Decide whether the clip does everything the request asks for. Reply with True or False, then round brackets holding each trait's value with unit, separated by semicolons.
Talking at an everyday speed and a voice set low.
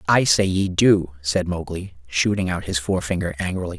True (175 wpm; 90 Hz)